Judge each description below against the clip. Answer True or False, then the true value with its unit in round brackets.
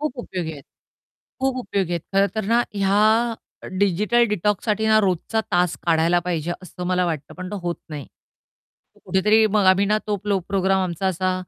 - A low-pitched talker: False (190 Hz)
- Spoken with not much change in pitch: False (3.2 semitones)